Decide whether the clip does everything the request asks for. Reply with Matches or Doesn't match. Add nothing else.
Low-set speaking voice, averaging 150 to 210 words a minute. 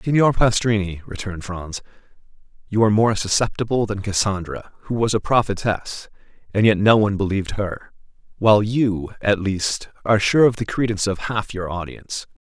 Matches